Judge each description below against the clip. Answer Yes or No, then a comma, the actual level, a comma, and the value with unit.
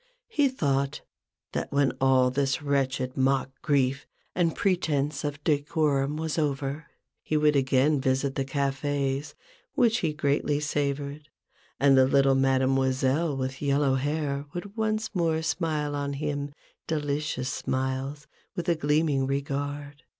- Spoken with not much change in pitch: Yes, narrow, 2.0 semitones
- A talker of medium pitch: Yes, medium, 145 Hz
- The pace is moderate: No, slow, 130 wpm